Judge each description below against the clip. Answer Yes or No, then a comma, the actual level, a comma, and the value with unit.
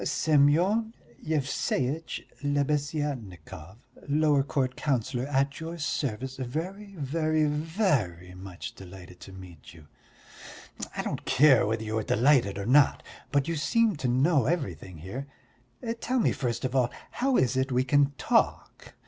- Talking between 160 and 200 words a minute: No, average, 140 wpm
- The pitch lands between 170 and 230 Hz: No, low, 135 Hz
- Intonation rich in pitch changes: Yes, wide, 5.7 semitones